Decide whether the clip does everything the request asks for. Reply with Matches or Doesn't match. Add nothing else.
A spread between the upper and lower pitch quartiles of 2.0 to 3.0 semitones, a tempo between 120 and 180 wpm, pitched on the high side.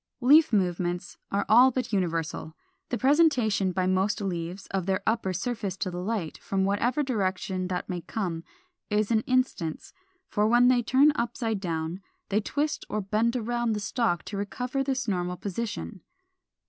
Doesn't match